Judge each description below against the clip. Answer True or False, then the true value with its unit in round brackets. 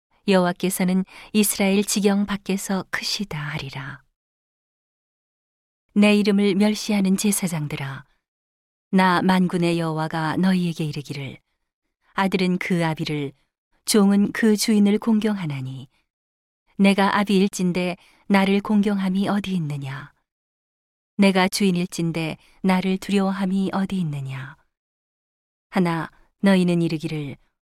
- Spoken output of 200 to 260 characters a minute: True (245 characters per minute)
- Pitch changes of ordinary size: True (4.1 semitones)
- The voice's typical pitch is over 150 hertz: True (185 Hz)